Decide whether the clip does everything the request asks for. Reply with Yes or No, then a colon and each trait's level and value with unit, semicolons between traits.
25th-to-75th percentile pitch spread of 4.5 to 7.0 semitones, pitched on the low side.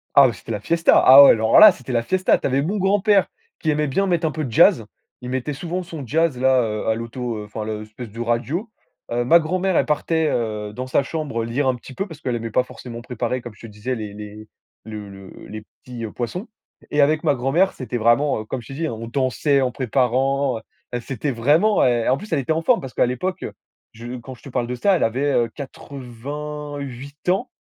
Yes: average, 4.8 semitones; low, 130 Hz